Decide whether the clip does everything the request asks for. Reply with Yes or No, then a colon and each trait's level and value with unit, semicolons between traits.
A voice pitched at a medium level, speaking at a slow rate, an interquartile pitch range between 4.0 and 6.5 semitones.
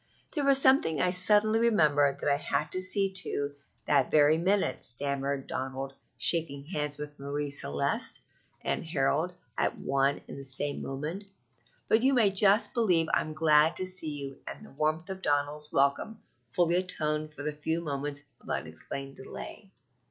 No: medium, 150 Hz; average, 165 wpm; average, 4.6 semitones